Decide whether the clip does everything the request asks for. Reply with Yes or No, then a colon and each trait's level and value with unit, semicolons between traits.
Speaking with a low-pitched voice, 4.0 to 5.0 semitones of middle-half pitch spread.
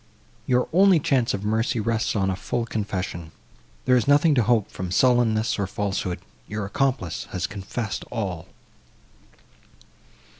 Yes: low, 110 Hz; average, 4.3 semitones